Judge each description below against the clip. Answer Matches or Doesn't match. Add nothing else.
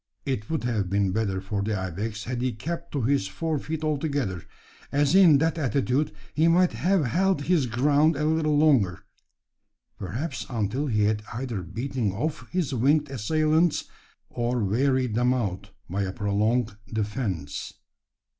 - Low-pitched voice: Matches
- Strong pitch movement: Matches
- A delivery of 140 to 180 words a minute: Matches